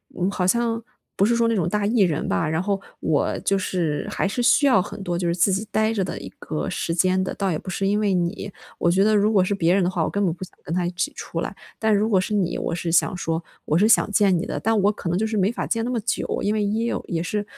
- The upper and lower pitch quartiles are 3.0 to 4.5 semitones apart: Yes, average, 3.3 semitones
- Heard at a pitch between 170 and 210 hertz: Yes, high, 195 Hz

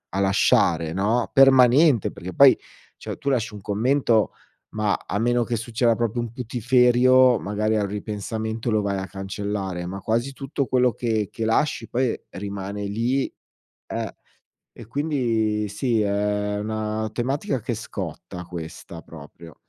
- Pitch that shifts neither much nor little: Yes, average, 3.3 semitones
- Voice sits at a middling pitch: No, low, 110 Hz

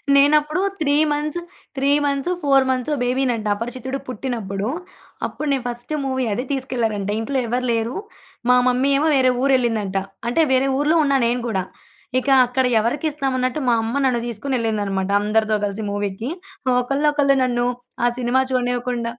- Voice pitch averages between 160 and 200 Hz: No, very high, 250 Hz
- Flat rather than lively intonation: No, average, 3.2 semitones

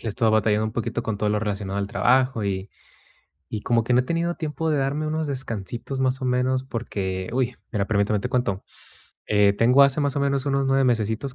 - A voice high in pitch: No, low, 120 Hz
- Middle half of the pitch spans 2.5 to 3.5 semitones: No, average, 4.3 semitones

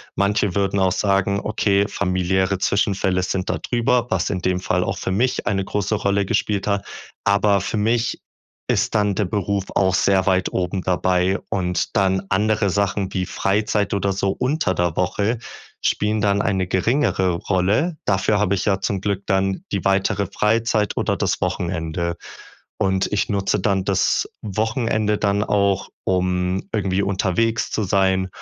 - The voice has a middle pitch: No, low, 100 Hz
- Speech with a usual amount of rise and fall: No, narrow, 1.8 semitones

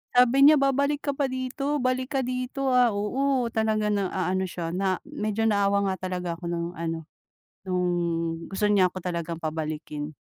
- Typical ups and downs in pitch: No, wide, 6.8 semitones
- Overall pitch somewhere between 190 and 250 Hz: Yes, high, 200 Hz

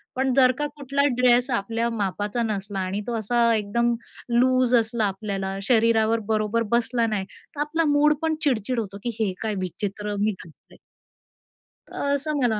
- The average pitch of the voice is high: Yes, high, 230 Hz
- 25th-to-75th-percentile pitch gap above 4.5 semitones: No, average, 3.4 semitones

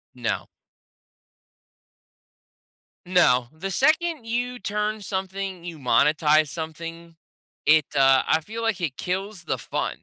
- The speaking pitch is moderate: Yes, medium, 175 Hz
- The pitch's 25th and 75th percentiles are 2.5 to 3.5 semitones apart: No, average, 5.1 semitones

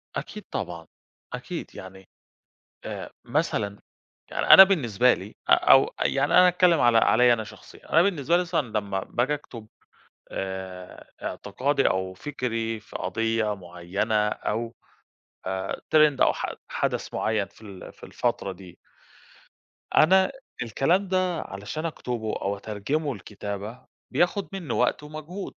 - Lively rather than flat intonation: Yes, wide, 7.4 semitones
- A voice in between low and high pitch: No, low, 115 Hz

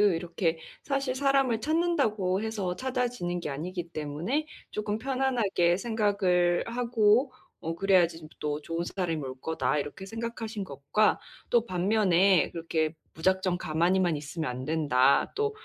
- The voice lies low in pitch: No, medium, 185 Hz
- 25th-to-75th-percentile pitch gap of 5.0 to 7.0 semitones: Yes, wide, 5.6 semitones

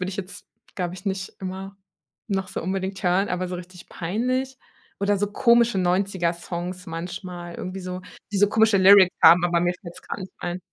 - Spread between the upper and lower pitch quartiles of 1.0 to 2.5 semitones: Yes, narrow, 1.9 semitones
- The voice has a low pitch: No, medium, 185 Hz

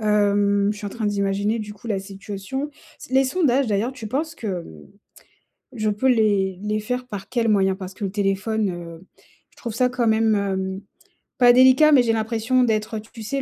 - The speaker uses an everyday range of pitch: Yes, average, 3.6 semitones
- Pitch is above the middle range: Yes, high, 215 Hz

